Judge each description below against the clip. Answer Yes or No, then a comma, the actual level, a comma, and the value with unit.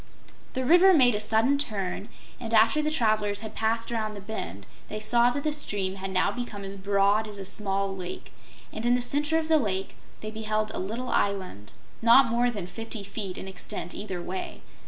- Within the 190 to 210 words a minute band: Yes, average, 200 wpm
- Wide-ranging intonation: No, average, 3.6 semitones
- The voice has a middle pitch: No, high, 215 Hz